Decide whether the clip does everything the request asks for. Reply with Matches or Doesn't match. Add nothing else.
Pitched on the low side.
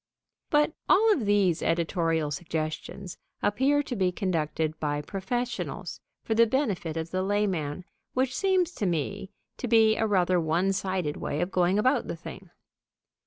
Doesn't match